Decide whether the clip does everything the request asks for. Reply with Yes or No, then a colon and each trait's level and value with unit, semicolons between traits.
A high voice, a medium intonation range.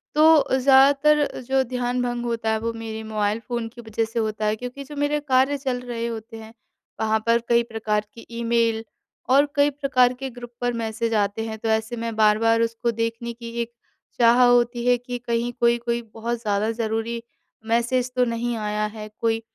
No: high, 235 Hz; narrow, 1.9 semitones